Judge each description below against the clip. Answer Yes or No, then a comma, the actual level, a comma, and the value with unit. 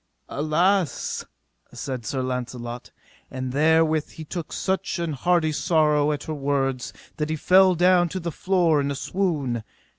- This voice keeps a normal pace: Yes, average, 150 wpm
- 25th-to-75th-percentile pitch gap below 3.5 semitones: No, average, 4.3 semitones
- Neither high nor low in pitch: Yes, medium, 155 Hz